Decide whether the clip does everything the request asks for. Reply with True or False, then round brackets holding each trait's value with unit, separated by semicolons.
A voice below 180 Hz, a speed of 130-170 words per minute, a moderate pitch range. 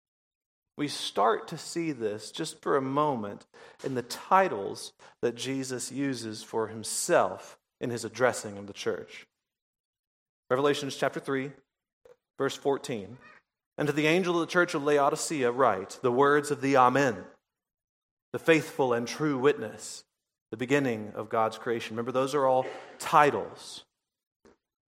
True (135 Hz; 140 wpm; 4.1 semitones)